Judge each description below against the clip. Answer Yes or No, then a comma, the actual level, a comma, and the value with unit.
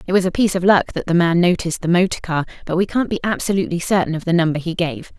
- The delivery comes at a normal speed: No, fast, 280 wpm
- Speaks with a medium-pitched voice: Yes, medium, 175 Hz